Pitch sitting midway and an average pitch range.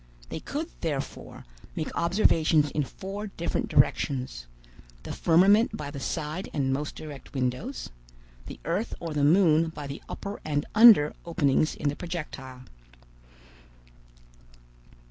Yes: medium, 155 Hz; average, 3.8 semitones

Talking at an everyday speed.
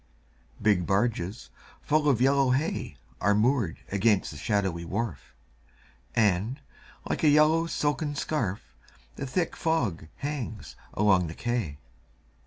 No: slow, 120 wpm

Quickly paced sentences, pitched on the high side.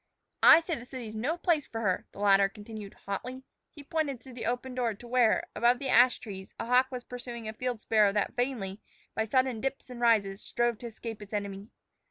Yes: fast, 215 wpm; high, 235 Hz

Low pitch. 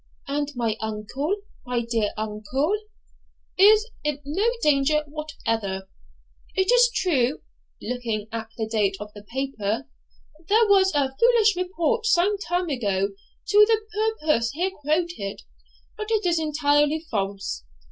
No: very high, 290 Hz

